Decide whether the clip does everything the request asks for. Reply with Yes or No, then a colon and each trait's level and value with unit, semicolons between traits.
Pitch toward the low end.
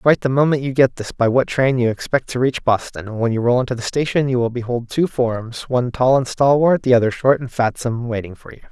Yes: low, 125 Hz